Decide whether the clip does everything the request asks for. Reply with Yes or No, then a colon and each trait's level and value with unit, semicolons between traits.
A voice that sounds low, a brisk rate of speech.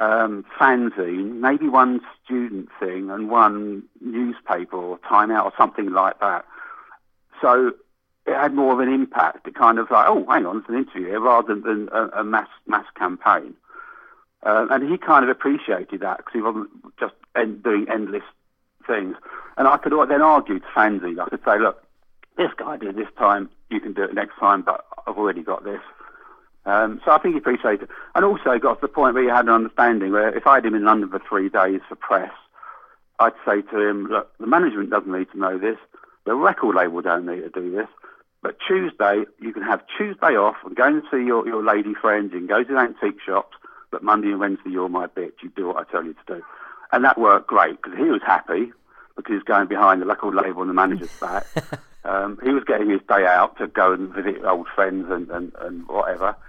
Yes: low, 110 Hz; fast, 215 wpm